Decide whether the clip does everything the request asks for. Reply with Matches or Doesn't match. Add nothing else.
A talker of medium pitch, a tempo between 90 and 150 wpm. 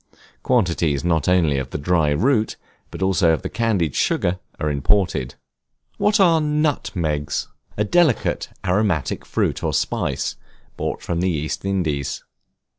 Doesn't match